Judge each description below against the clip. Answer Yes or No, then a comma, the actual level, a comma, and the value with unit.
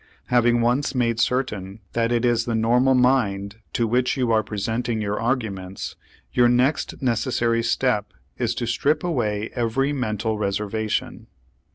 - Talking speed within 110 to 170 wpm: Yes, average, 145 wpm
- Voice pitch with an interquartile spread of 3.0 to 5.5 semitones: No, narrow, 2.5 semitones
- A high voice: No, low, 115 Hz